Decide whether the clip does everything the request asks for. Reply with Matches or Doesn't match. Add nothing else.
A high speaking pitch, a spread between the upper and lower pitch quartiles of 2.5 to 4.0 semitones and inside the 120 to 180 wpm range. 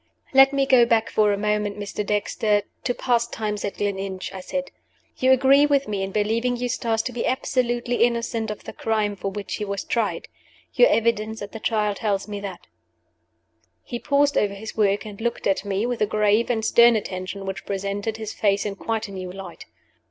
Doesn't match